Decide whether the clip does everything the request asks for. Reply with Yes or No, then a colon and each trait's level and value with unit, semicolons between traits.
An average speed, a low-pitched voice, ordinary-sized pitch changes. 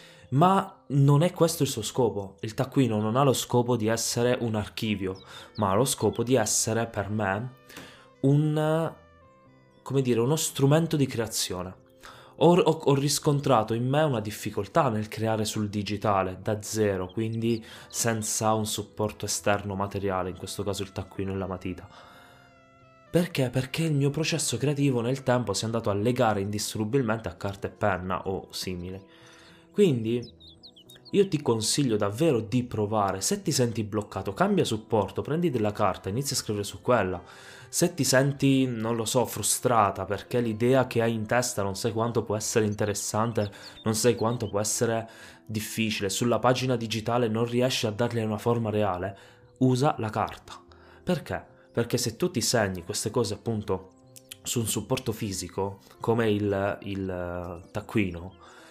Yes: average, 160 wpm; low, 110 Hz; average, 4.1 semitones